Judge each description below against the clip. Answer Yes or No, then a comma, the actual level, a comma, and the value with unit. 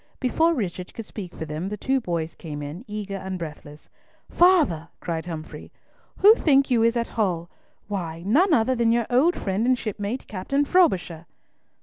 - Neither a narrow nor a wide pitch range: No, wide, 7.0 semitones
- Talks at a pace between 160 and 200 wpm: Yes, average, 170 wpm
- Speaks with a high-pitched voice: Yes, high, 205 Hz